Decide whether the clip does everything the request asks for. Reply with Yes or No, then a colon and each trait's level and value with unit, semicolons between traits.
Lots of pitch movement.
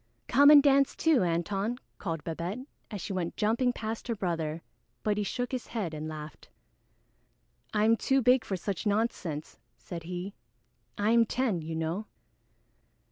Yes: wide, 5.7 semitones